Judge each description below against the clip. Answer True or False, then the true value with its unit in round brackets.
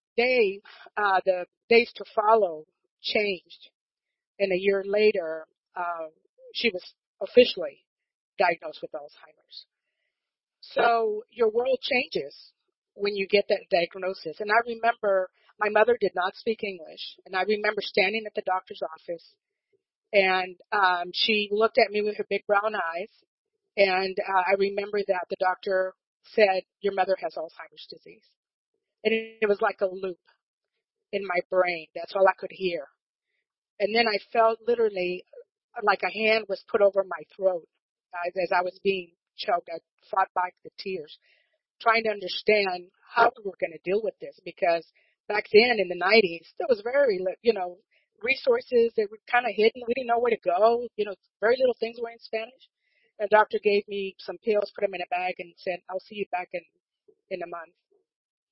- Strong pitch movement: False (4.3 semitones)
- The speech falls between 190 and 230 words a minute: False (175 wpm)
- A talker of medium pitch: False (210 Hz)